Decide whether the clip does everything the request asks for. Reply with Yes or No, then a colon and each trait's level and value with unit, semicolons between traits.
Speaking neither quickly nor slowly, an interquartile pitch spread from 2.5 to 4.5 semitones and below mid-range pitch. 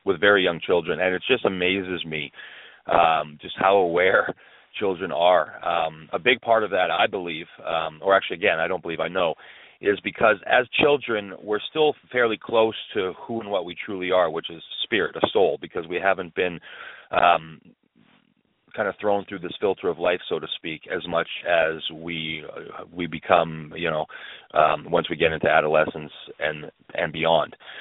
No: average, 185 wpm; average, 5.3 semitones; very low, 95 Hz